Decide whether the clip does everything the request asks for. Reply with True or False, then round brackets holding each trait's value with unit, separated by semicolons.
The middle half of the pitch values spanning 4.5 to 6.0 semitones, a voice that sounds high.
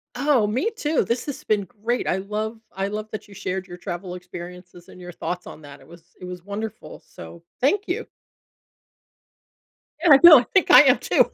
True (5.1 semitones; 200 Hz)